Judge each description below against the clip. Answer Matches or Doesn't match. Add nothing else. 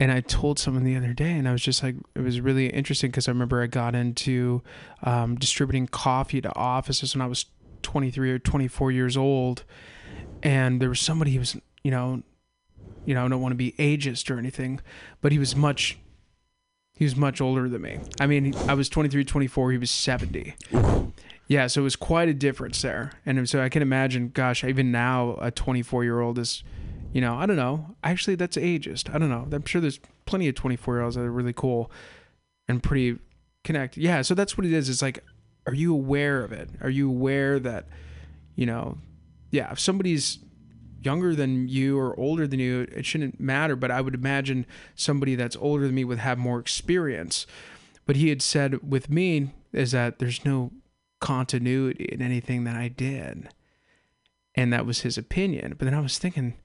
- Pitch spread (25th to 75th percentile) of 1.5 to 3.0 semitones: Matches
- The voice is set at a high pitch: Doesn't match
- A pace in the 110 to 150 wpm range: Doesn't match